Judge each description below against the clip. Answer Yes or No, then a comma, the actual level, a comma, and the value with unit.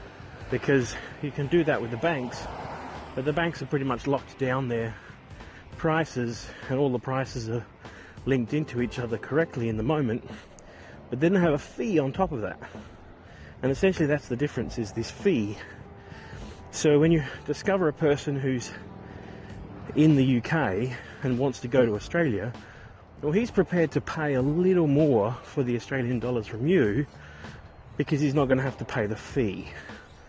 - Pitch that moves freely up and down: No, average, 4.8 semitones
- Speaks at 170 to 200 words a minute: Yes, average, 175 wpm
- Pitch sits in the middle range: No, low, 130 Hz